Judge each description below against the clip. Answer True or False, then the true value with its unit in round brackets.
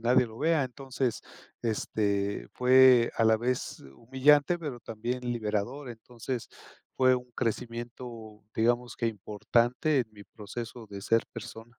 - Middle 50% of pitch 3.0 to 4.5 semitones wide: False (2.4 semitones)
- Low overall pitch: True (120 Hz)